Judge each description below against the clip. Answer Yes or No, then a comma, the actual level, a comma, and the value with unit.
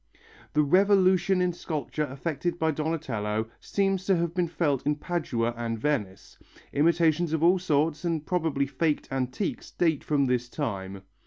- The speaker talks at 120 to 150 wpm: Yes, average, 145 wpm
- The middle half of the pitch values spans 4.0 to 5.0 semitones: Yes, average, 4.5 semitones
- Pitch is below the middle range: No, medium, 155 Hz